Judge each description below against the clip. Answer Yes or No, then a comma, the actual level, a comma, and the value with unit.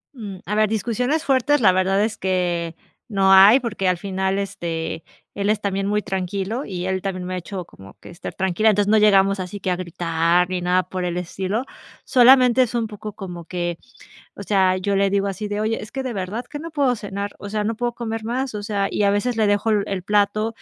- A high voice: Yes, high, 200 Hz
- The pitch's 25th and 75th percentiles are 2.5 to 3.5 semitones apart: Yes, average, 2.9 semitones